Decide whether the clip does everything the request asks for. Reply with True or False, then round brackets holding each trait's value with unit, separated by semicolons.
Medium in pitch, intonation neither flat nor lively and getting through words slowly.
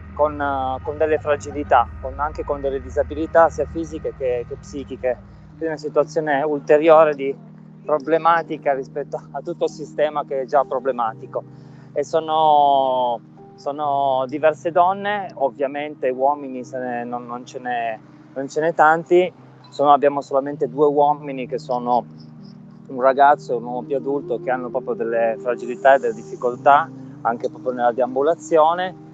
False (145 Hz; 3.1 semitones; 145 wpm)